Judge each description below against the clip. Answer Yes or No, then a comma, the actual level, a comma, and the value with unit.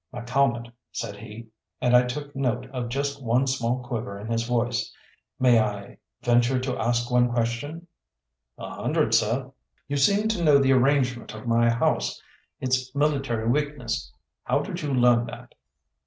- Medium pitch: No, low, 125 Hz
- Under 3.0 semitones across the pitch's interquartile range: Yes, narrow, 2.6 semitones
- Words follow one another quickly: No, average, 155 wpm